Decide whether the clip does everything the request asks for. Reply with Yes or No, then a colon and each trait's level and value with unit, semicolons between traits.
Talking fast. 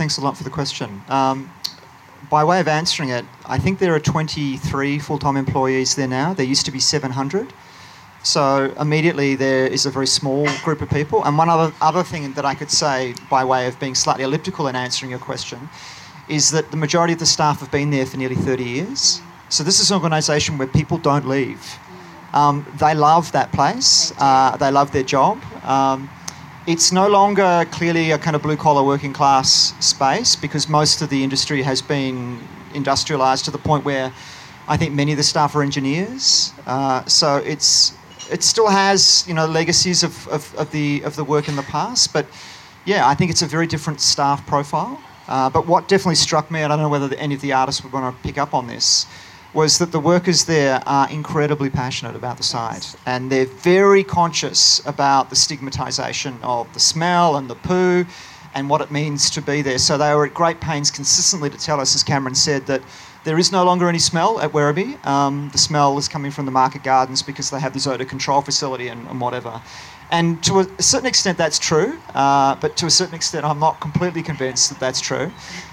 Yes: fast, 210 wpm